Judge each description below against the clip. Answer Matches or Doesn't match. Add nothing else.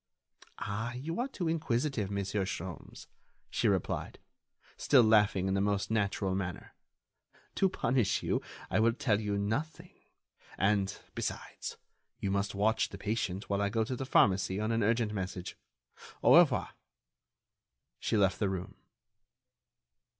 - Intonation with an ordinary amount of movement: Matches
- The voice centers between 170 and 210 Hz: Doesn't match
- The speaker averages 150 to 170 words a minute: Doesn't match